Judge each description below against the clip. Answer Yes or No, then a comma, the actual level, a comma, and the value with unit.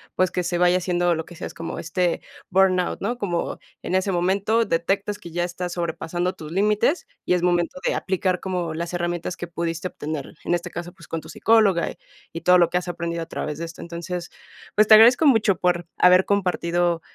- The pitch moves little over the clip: Yes, narrow, 1.9 semitones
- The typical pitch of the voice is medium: Yes, medium, 175 Hz